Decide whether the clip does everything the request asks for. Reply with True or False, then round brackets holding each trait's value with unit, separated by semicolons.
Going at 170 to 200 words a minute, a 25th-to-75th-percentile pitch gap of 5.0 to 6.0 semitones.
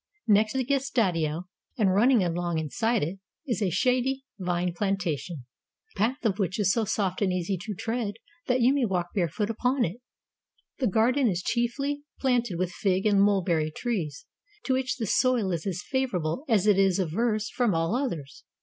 True (180 wpm; 5.4 semitones)